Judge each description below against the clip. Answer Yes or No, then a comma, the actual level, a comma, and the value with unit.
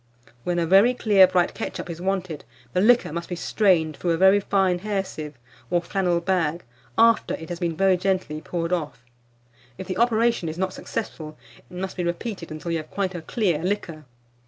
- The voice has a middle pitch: Yes, medium, 180 Hz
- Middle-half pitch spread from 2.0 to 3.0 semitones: Yes, narrow, 2.6 semitones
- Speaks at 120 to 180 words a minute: No, average, 195 wpm